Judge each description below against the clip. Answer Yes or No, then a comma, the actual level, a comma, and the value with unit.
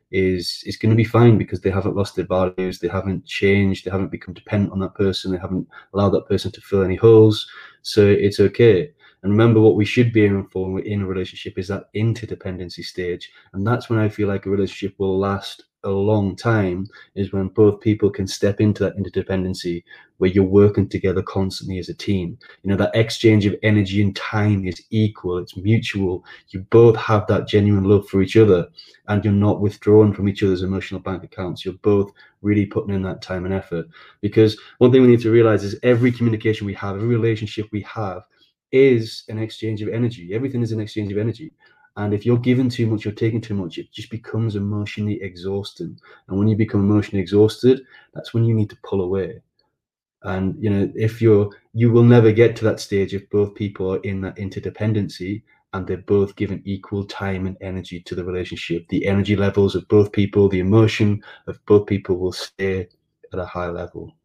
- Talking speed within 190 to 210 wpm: Yes, fast, 205 wpm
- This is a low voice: Yes, low, 100 Hz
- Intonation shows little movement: Yes, narrow, 2.3 semitones